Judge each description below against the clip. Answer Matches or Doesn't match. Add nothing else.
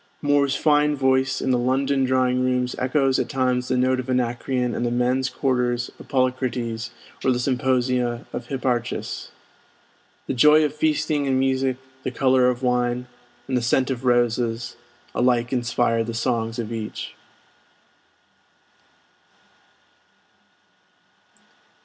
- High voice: Doesn't match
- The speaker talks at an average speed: Doesn't match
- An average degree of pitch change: Doesn't match